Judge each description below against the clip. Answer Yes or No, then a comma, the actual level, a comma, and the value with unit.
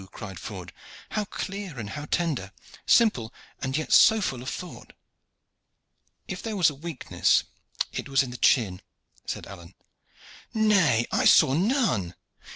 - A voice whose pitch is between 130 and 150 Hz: Yes, medium, 140 Hz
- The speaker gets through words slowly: No, average, 145 wpm